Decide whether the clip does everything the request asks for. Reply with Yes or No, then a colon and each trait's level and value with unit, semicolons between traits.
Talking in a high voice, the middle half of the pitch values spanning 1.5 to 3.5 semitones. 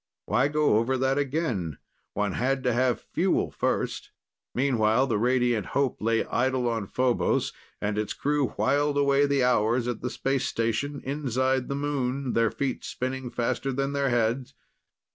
No: low, 130 Hz; average, 2.8 semitones